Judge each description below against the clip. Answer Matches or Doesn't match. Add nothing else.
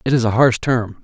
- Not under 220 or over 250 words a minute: Doesn't match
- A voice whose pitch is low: Matches